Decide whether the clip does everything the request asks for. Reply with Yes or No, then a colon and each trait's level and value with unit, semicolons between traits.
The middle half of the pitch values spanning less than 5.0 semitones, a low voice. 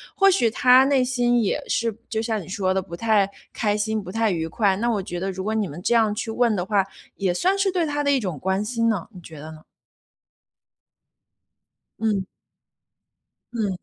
No: average, 4.0 semitones; high, 215 Hz